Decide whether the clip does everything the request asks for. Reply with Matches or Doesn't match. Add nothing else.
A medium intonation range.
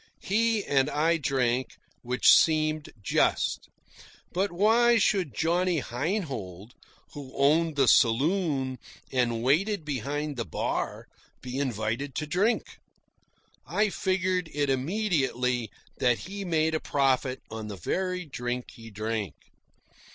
Doesn't match